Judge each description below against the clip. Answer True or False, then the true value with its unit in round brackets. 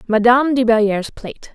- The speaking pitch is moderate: False (230 Hz)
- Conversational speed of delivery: True (155 wpm)